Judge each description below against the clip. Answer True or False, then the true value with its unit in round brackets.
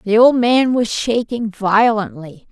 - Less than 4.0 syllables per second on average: True (3.7 syllables/s)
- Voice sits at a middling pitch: False (220 Hz)